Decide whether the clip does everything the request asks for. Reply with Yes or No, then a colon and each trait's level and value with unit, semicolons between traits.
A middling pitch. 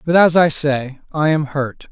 Yes: medium, 150 Hz